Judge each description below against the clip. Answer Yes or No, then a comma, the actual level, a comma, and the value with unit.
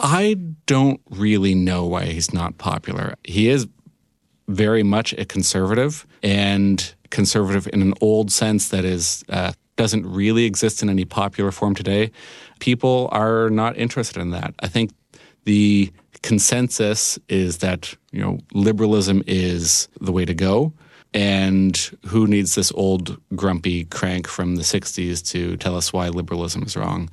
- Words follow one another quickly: No, average, 150 wpm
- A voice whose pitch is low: Yes, low, 100 Hz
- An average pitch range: Yes, average, 3.2 semitones